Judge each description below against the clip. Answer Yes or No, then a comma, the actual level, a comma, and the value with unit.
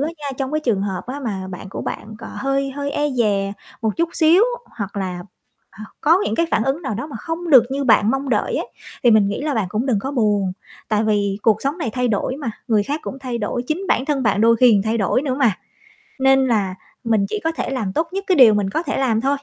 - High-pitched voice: Yes, high, 245 Hz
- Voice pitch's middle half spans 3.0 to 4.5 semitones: No, average, 5.1 semitones